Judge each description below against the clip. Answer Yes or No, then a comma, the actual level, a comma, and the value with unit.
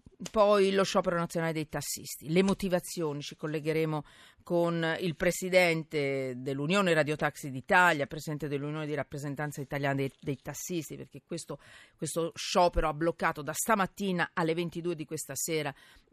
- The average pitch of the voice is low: No, medium, 160 Hz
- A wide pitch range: No, average, 3.1 semitones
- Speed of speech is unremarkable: Yes, average, 140 wpm